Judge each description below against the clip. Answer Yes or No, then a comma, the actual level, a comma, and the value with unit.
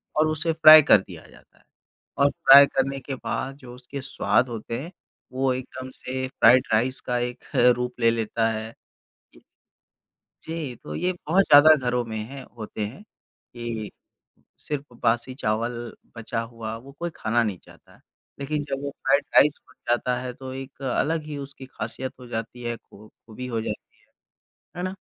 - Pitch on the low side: Yes, low, 130 Hz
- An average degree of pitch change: Yes, average, 3.3 semitones